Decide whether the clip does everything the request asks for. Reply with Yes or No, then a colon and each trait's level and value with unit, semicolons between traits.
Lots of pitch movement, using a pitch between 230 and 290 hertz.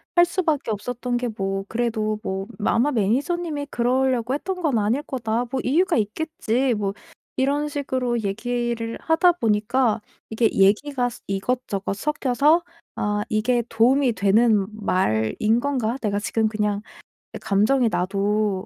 No: average, 4.3 semitones; high, 235 Hz